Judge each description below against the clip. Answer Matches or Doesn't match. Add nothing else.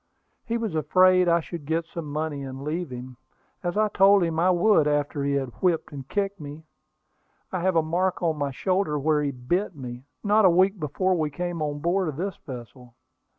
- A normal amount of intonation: Matches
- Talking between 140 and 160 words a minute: Doesn't match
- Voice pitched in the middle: Matches